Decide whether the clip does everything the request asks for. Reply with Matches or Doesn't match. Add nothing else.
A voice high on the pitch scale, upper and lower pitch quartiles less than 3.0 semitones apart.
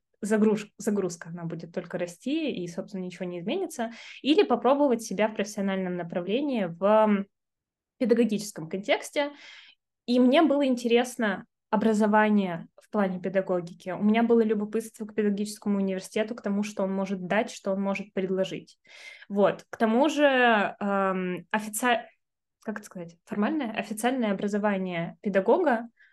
Doesn't match